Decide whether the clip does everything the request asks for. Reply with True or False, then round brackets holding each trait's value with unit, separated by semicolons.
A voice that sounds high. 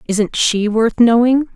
True (230 Hz)